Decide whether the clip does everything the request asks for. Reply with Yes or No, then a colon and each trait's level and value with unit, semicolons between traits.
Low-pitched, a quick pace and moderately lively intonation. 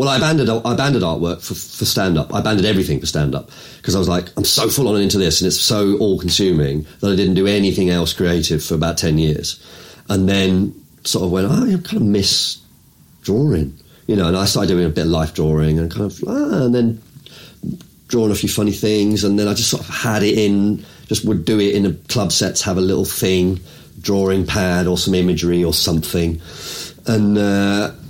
Yes: very low, 95 Hz; fast, 225 wpm; average, 3.3 semitones